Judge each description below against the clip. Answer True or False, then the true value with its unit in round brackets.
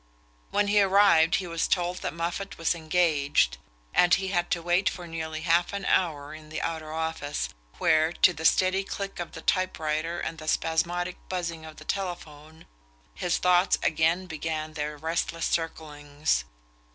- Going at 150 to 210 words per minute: True (165 wpm)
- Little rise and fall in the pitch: True (2.3 semitones)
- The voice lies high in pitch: False (165 Hz)